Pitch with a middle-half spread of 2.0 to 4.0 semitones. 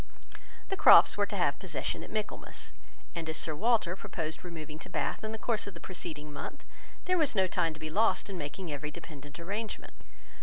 No: average, 4.8 semitones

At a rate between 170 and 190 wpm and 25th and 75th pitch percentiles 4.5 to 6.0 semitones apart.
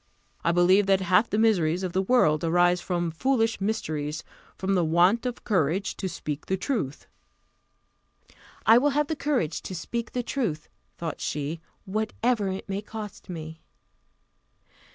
No: average, 155 wpm; average, 5.1 semitones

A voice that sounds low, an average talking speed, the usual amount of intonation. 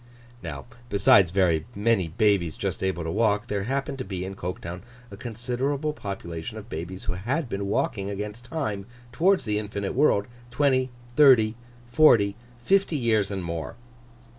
Yes: low, 105 Hz; average, 155 wpm; average, 4.4 semitones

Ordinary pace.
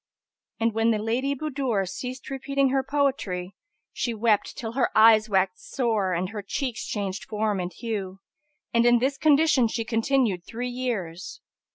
Yes: average, 160 wpm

